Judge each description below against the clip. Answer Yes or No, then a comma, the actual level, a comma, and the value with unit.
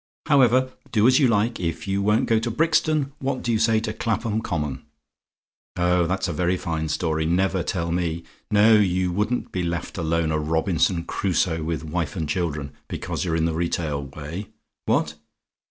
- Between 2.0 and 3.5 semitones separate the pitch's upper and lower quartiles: No, average, 5.2 semitones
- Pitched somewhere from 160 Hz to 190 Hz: No, very low, 90 Hz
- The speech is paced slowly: No, average, 180 wpm